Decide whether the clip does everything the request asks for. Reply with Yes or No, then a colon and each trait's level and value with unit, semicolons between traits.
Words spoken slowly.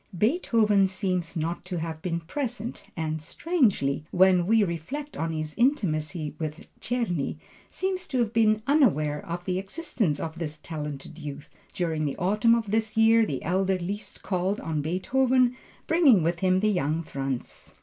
No: average, 160 wpm